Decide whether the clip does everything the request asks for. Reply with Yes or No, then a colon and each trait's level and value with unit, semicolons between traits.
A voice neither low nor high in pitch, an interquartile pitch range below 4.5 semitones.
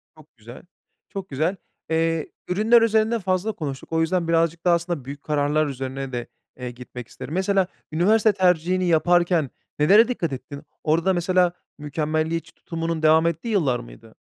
Yes: medium, 165 Hz; average, 3.8 semitones